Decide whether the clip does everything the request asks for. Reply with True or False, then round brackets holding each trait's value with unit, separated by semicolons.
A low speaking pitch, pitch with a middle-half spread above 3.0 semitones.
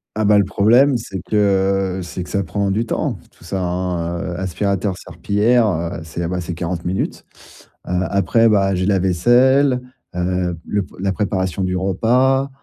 False (95 Hz; 2.7 semitones)